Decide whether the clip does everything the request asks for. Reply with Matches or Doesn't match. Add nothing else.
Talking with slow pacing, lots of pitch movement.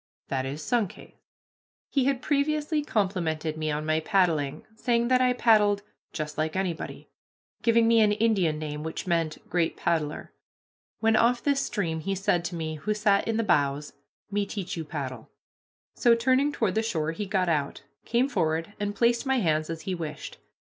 Doesn't match